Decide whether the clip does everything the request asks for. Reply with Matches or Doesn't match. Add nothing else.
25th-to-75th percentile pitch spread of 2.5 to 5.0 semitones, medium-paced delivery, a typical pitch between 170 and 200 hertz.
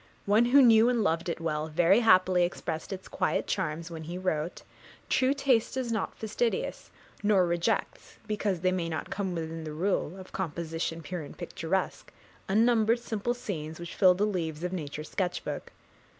Matches